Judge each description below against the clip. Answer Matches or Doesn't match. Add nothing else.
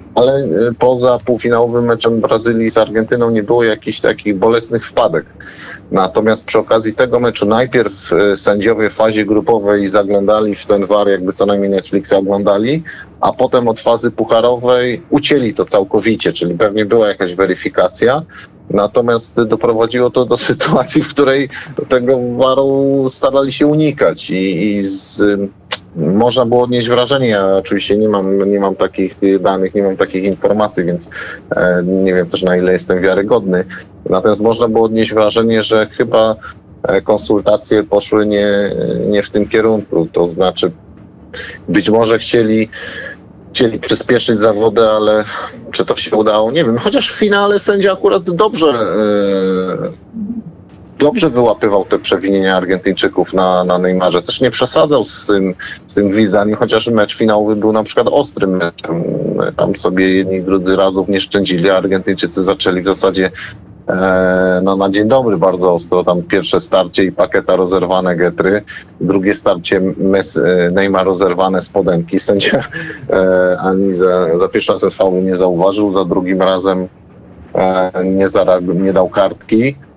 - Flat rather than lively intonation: Doesn't match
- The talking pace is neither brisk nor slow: Matches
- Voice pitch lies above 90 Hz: Matches